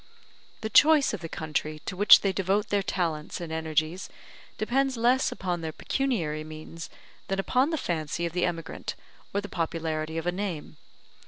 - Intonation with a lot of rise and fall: No, average, 4.3 semitones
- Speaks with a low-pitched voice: No, medium, 175 Hz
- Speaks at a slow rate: No, average, 170 wpm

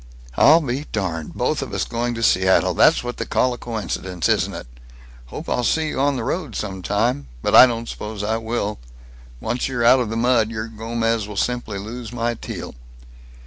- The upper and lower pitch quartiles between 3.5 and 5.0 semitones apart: No, narrow, 2.6 semitones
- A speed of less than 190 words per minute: No, average, 200 wpm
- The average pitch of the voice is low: Yes, low, 115 Hz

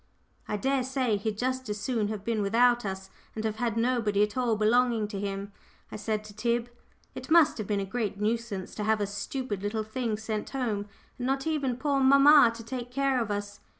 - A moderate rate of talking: No, fast, 215 wpm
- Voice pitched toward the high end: Yes, high, 225 Hz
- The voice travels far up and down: No, average, 3.4 semitones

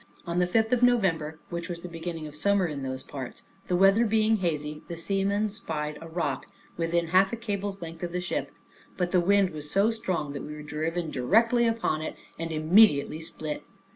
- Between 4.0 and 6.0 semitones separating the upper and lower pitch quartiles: Yes, average, 4.5 semitones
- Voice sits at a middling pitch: Yes, medium, 170 Hz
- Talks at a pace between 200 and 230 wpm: Yes, fast, 205 wpm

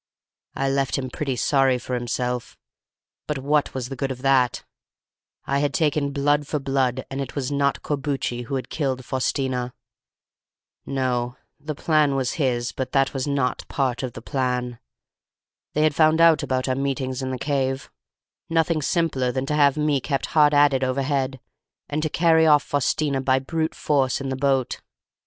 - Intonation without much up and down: Yes, narrow, 2.1 semitones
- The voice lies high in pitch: No, low, 135 Hz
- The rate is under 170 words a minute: No, average, 175 wpm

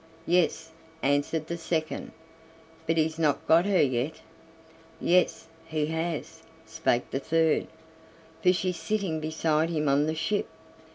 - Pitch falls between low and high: Yes, medium, 160 Hz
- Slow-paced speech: Yes, slow, 130 wpm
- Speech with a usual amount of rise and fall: No, narrow, 1.8 semitones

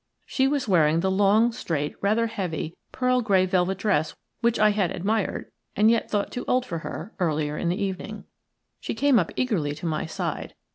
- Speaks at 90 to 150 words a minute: No, average, 190 wpm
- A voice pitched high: Yes, high, 195 Hz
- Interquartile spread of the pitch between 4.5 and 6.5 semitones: Yes, average, 5.0 semitones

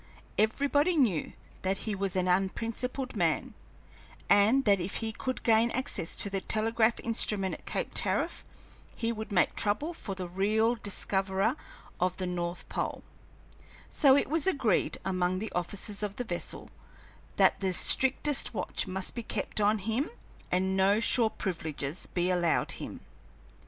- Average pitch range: Yes, average, 3.8 semitones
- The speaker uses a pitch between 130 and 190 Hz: No, high, 205 Hz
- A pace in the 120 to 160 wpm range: Yes, average, 150 wpm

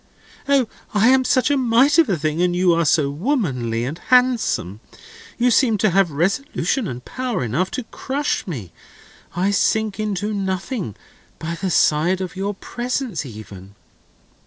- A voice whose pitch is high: Yes, high, 195 Hz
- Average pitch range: No, wide, 7.9 semitones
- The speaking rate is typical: Yes, average, 160 wpm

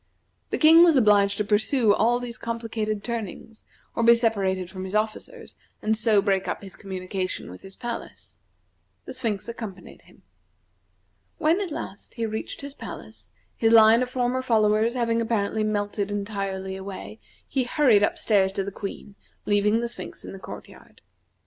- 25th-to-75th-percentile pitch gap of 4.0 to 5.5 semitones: No, average, 2.9 semitones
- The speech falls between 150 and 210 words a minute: Yes, average, 170 wpm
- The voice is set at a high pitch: Yes, high, 215 Hz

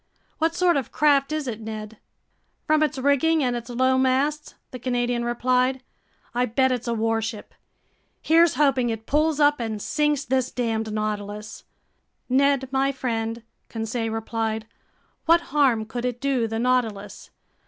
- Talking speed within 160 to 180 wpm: No, average, 150 wpm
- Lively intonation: No, average, 3.8 semitones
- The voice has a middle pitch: No, very high, 250 Hz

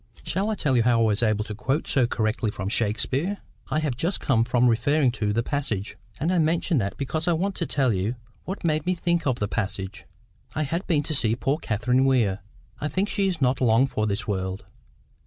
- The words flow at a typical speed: No, fast, 225 wpm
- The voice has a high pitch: No, low, 130 Hz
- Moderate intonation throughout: No, wide, 6.2 semitones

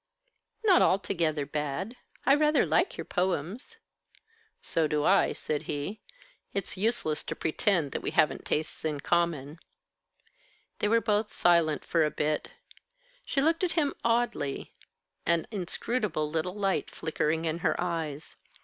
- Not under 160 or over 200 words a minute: No, average, 140 wpm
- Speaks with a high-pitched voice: No, medium, 170 Hz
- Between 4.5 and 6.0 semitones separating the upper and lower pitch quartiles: Yes, wide, 5.6 semitones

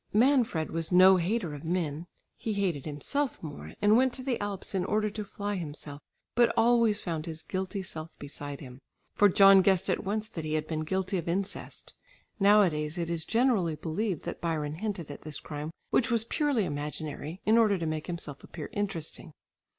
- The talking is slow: No, average, 190 wpm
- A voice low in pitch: No, medium, 180 Hz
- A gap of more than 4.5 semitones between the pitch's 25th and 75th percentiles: Yes, average, 5.0 semitones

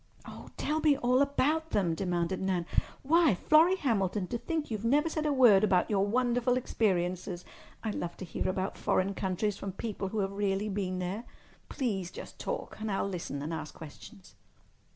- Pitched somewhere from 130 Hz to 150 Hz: No, high, 205 Hz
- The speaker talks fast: No, average, 175 wpm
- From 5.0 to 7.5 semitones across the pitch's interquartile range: Yes, average, 5.3 semitones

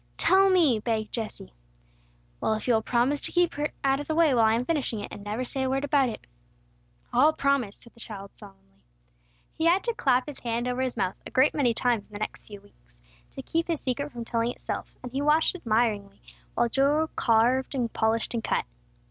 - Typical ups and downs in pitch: Yes, average, 4.5 semitones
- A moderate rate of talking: No, fast, 225 wpm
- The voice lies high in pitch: Yes, high, 245 Hz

